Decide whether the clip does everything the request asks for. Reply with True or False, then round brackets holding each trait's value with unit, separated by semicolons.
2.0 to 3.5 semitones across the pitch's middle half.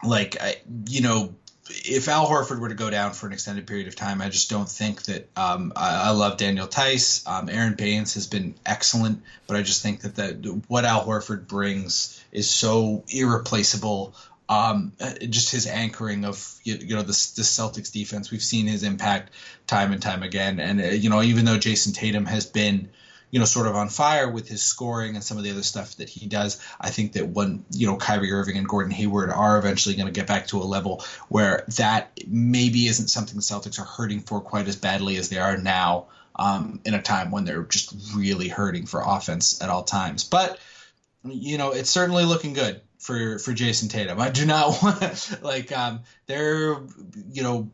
True (2.9 semitones)